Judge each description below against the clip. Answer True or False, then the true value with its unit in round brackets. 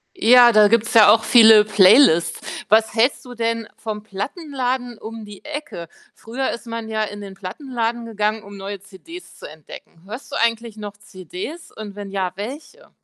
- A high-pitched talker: True (220 Hz)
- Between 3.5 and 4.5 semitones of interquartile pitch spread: False (3.1 semitones)